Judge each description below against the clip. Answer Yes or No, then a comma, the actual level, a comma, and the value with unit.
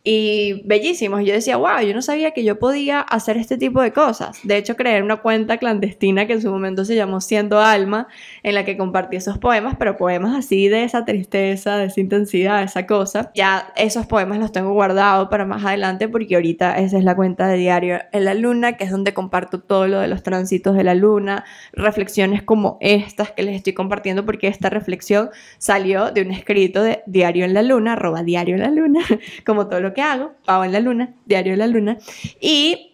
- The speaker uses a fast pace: Yes, fast, 215 wpm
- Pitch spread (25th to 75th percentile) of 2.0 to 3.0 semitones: Yes, narrow, 2.5 semitones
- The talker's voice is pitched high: Yes, high, 205 Hz